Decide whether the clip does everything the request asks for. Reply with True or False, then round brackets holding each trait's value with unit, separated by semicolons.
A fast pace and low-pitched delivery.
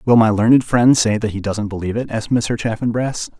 True (230 wpm; 110 Hz)